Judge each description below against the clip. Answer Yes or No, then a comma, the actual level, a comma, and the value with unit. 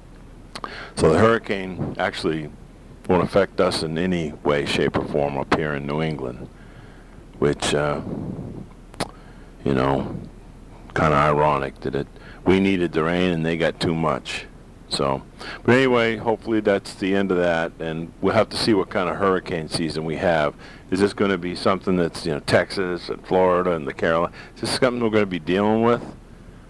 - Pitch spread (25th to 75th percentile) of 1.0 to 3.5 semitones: No, average, 4.1 semitones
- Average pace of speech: Yes, average, 180 wpm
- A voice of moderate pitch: No, very low, 90 Hz